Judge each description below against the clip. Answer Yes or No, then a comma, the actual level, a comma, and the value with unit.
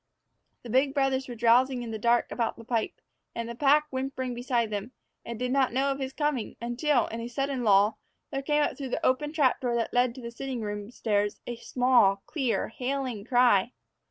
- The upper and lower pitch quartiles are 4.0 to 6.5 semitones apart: No, narrow, 2.5 semitones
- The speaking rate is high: Yes, fast, 210 wpm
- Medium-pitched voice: No, high, 245 Hz